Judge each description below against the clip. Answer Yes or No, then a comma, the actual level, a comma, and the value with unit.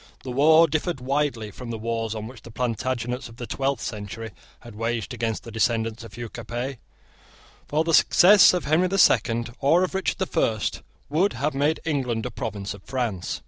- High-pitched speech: No, low, 120 Hz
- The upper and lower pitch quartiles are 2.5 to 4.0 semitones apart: No, average, 4.6 semitones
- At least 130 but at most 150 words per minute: No, average, 185 wpm